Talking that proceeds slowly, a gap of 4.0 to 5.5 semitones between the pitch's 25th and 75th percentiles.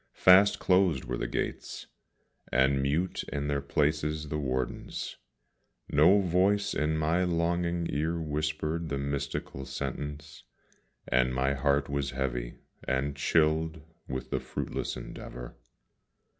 No: slow, 120 wpm; average, 3.3 semitones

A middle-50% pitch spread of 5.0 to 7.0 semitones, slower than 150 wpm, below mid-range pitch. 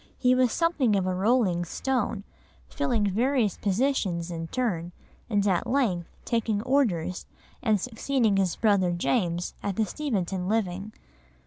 No: wide, 5.4 semitones; slow, 135 wpm; high, 205 Hz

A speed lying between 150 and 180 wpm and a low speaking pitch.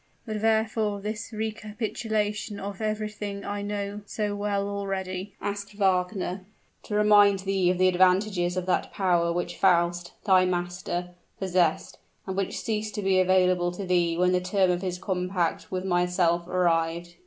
No: average, 155 wpm; high, 190 Hz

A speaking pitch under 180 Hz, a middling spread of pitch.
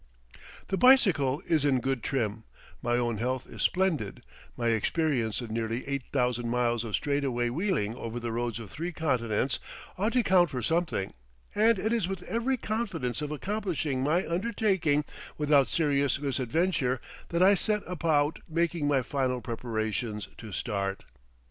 No: medium, 140 Hz; wide, 6.5 semitones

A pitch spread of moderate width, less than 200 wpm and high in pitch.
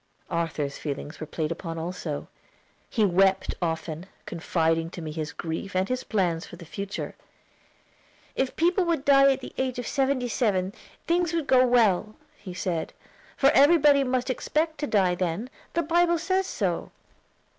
No: wide, 8.5 semitones; average, 160 wpm; high, 205 Hz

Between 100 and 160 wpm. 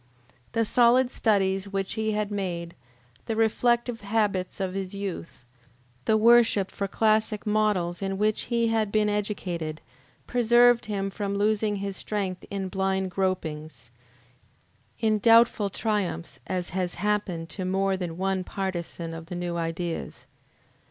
Yes: average, 140 wpm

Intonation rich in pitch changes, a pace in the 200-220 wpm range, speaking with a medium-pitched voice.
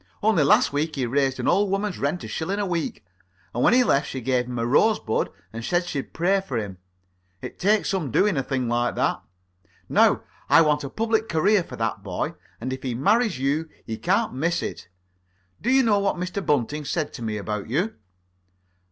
Yes: wide, 7.9 semitones; fast, 205 wpm; medium, 150 Hz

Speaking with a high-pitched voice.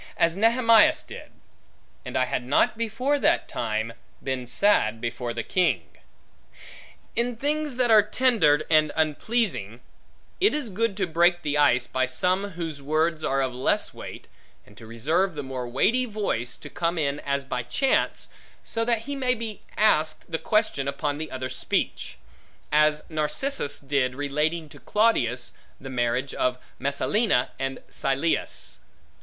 No: medium, 155 Hz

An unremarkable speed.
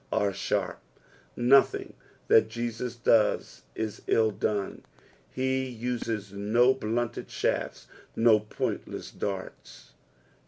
No: slow, 95 wpm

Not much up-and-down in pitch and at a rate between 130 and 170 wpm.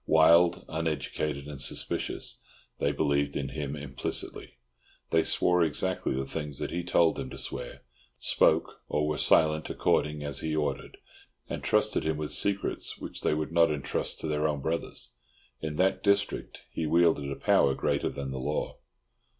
Yes: narrow, 2.3 semitones; average, 165 wpm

